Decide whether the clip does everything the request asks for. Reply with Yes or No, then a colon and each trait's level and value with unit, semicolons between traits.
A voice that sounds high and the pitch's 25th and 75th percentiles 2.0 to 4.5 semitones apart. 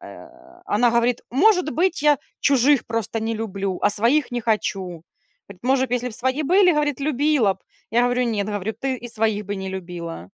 No: high, 235 Hz; average, 5.1 semitones